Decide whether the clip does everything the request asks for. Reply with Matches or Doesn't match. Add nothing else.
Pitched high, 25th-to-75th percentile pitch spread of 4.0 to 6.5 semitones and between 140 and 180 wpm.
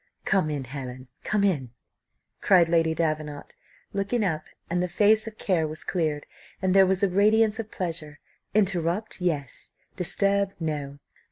Doesn't match